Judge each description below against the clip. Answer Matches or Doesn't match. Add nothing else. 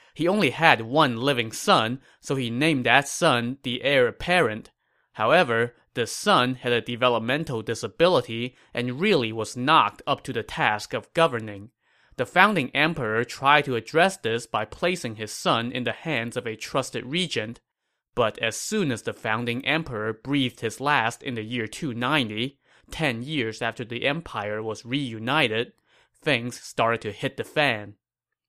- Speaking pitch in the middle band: Doesn't match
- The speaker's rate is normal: Matches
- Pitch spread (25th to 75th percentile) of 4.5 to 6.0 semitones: Doesn't match